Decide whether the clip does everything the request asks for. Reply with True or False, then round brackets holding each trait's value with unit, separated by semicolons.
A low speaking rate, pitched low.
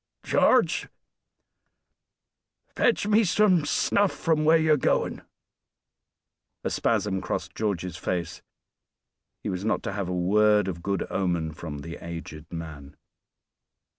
True (120 wpm; 95 Hz)